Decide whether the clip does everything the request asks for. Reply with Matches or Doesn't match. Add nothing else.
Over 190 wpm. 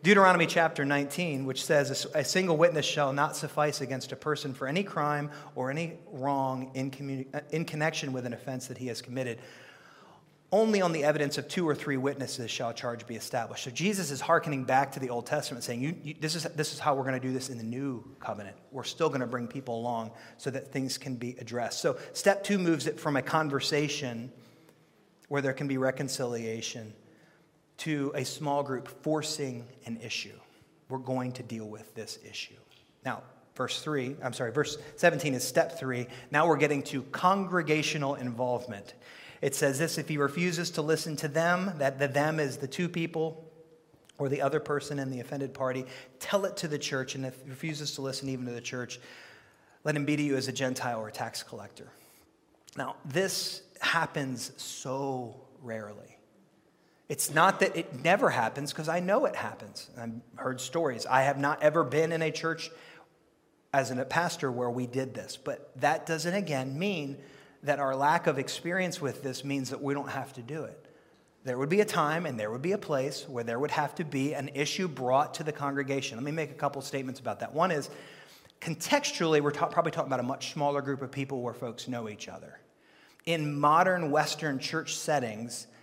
Matches